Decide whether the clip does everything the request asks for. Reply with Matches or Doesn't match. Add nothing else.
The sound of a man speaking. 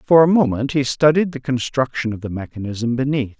Matches